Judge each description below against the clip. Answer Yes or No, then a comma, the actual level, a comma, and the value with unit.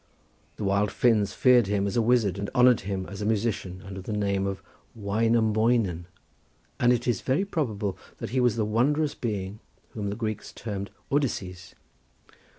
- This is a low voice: Yes, low, 105 Hz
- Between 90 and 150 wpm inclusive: No, average, 165 wpm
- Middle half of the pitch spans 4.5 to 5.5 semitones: No, average, 3.3 semitones